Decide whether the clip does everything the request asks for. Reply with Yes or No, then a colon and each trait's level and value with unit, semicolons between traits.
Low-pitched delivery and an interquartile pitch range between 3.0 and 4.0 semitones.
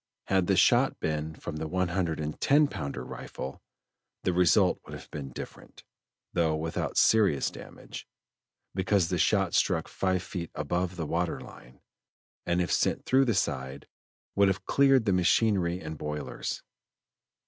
Yes: very low, 85 Hz; average, 3.7 semitones